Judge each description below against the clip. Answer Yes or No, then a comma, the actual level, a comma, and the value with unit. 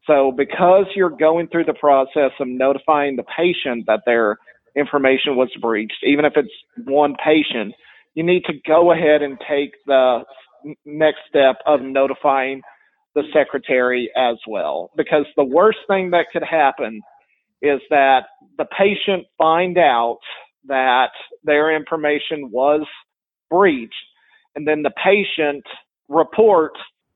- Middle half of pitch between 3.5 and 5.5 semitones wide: Yes, average, 3.8 semitones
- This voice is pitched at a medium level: Yes, medium, 150 Hz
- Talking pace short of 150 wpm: Yes, slow, 135 wpm